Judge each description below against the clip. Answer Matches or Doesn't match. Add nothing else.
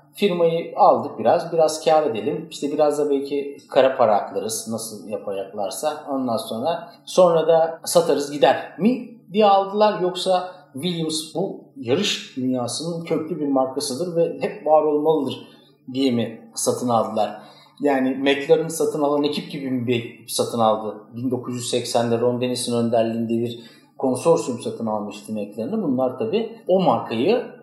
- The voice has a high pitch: Doesn't match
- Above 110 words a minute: Matches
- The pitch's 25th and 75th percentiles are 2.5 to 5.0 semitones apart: Doesn't match